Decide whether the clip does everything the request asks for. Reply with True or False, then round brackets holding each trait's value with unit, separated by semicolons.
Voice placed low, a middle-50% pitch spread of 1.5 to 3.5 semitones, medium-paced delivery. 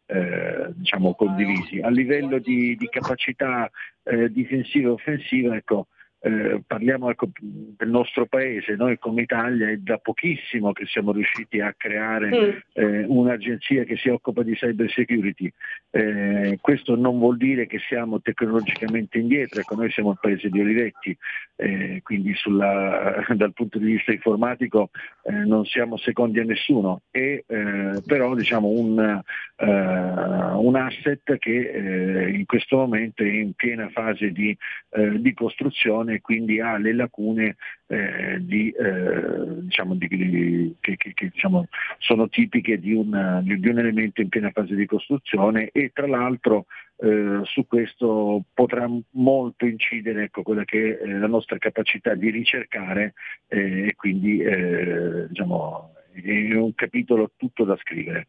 True (110 Hz; 2.8 semitones; 135 wpm)